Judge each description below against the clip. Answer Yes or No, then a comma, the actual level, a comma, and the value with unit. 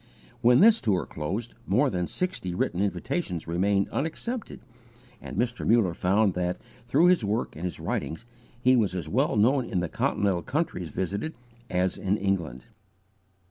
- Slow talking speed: No, average, 155 wpm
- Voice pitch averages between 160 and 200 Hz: No, low, 100 Hz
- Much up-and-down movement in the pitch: Yes, wide, 5.8 semitones